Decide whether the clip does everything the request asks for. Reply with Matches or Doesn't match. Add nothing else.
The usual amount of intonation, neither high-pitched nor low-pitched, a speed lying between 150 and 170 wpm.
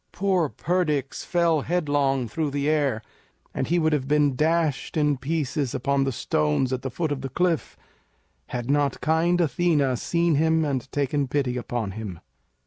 Matches